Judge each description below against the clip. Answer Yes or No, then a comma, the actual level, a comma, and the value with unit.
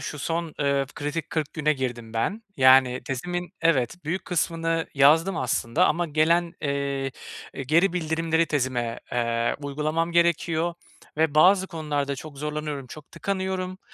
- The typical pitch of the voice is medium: Yes, medium, 155 Hz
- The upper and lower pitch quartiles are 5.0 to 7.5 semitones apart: No, average, 3.4 semitones